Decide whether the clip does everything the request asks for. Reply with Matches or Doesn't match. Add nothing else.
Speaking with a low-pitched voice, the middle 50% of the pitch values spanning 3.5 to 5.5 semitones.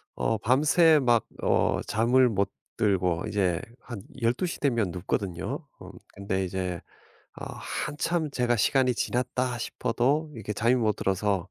Matches